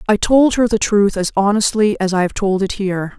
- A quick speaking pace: Yes, fast, 245 wpm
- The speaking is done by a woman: Yes, female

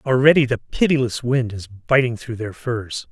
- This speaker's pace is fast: No, average, 175 wpm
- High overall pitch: No, low, 120 Hz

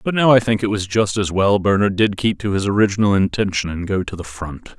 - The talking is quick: Yes, fast, 265 wpm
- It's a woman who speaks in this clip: No, male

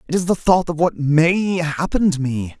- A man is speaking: Yes, male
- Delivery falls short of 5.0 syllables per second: Yes, 4.5 syllables/s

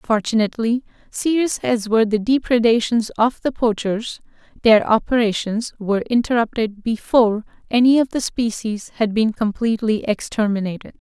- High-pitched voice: Yes, high, 225 Hz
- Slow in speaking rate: Yes, slow, 120 wpm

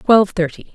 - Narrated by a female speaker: Yes, female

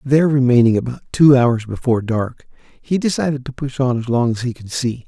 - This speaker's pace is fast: Yes, fast, 215 wpm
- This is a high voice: No, low, 130 Hz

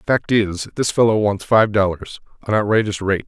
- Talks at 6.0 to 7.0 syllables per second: No, 4.9 syllables/s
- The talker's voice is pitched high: No, low, 105 Hz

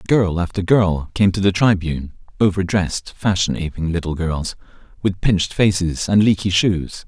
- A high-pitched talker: No, very low, 95 Hz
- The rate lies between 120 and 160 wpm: Yes, average, 155 wpm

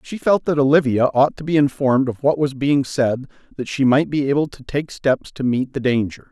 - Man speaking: Yes, male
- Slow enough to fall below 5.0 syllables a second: No, 5.3 syllables/s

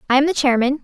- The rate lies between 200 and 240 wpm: No, fast, 285 wpm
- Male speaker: No, female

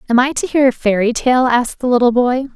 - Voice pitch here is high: Yes, very high, 250 Hz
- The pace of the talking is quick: Yes, fast, 260 wpm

